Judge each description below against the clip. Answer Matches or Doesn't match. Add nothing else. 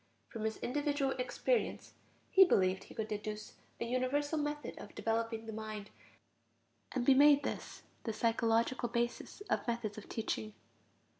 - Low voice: Doesn't match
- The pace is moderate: Matches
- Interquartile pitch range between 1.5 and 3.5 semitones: Doesn't match